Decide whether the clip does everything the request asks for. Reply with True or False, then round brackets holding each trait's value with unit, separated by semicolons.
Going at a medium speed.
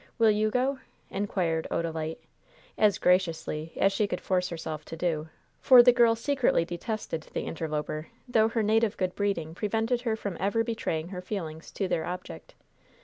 True (165 wpm)